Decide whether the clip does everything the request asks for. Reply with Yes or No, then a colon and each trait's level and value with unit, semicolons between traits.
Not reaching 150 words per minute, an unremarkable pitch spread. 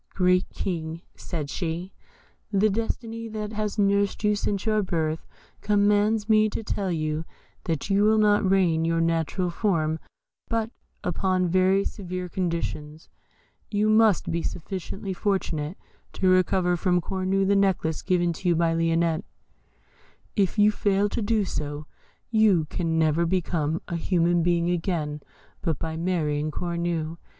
Yes: average, 140 wpm; average, 3.6 semitones